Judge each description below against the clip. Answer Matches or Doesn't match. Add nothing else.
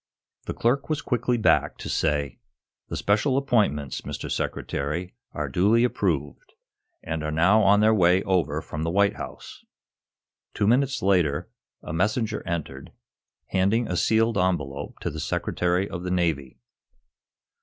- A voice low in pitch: Matches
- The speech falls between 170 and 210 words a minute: Doesn't match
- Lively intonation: Matches